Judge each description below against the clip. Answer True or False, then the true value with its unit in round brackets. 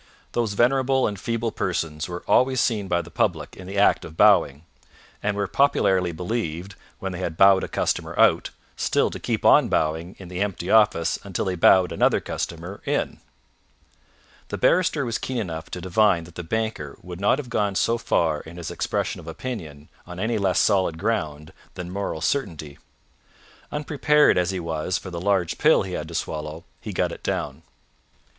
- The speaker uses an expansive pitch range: False (4.6 semitones)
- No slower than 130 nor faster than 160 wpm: False (185 wpm)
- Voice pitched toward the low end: True (95 Hz)